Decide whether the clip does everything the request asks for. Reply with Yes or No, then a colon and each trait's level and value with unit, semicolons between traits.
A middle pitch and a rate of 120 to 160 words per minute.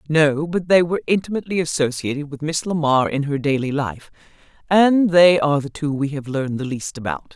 No: medium, 150 Hz; average, 195 wpm